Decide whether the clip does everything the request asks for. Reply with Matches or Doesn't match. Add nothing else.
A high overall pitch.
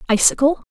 Matches